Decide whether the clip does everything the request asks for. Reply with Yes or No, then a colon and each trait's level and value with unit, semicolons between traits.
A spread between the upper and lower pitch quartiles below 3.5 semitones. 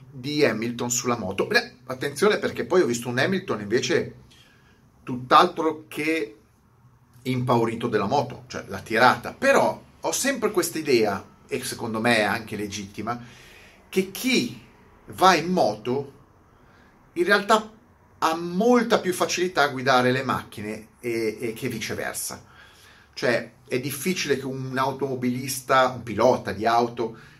No: wide, 5.5 semitones